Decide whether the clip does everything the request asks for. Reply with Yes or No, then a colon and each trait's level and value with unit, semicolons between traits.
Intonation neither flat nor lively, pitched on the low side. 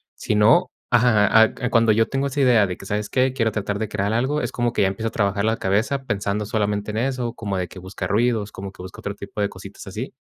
Yes: average, 3.0 semitones; low, 110 Hz